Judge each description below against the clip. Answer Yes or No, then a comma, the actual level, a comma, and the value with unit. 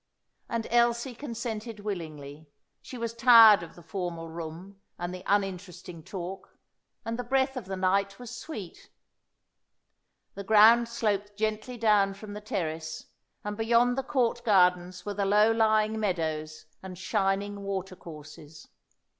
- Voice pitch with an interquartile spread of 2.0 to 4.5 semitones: Yes, average, 4.2 semitones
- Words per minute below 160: Yes, average, 140 wpm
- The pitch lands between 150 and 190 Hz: No, high, 200 Hz